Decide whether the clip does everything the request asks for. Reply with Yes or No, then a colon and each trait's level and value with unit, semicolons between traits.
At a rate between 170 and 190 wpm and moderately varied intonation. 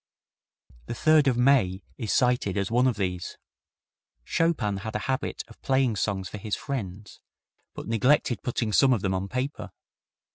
No: average, 160 wpm; average, 4.9 semitones